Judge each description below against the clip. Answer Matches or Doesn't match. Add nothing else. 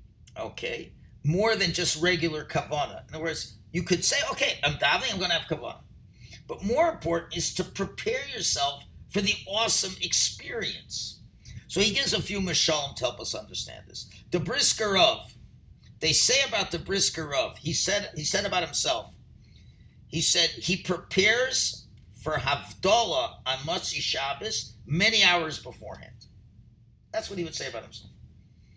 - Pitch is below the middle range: Doesn't match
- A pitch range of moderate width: Doesn't match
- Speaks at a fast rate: Doesn't match